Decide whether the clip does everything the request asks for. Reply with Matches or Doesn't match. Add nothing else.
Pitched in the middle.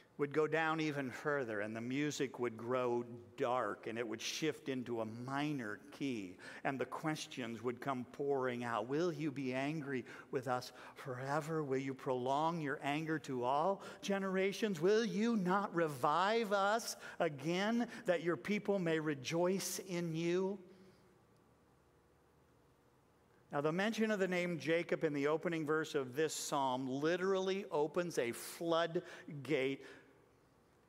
Matches